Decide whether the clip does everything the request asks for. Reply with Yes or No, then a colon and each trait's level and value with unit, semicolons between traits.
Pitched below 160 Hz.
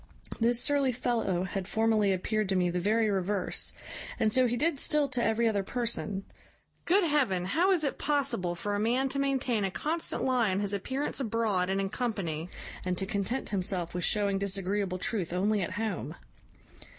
No: high, 210 Hz